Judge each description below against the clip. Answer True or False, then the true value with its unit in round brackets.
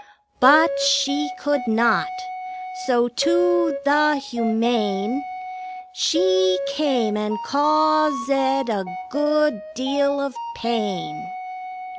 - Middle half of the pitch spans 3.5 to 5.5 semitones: True (4.4 semitones)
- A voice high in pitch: True (270 Hz)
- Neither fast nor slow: False (90 wpm)